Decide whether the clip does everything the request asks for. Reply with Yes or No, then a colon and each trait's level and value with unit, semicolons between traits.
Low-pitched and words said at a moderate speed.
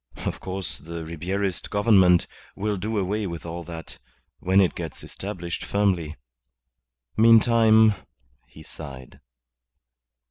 No: very low, 95 Hz; slow, 115 wpm